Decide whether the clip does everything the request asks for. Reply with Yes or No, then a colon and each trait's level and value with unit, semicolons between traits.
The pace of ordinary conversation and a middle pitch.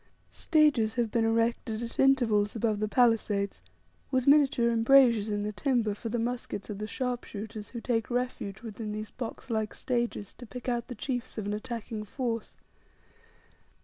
No: average, 165 wpm; high, 230 Hz